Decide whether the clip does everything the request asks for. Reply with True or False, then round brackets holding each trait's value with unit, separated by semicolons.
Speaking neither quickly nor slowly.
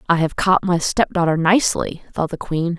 False (215 wpm)